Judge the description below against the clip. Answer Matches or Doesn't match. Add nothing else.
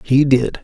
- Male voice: Matches